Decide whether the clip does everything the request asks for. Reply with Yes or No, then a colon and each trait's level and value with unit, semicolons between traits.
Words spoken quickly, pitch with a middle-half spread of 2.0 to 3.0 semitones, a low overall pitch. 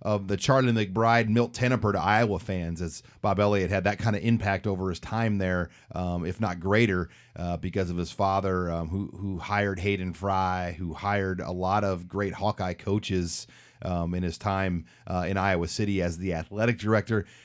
No: average, 195 wpm; narrow, 2.6 semitones; very low, 95 Hz